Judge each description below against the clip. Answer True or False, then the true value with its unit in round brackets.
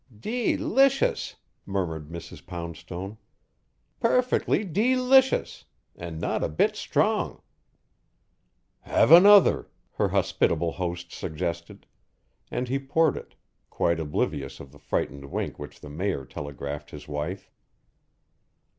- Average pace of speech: False (110 wpm)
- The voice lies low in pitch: True (85 Hz)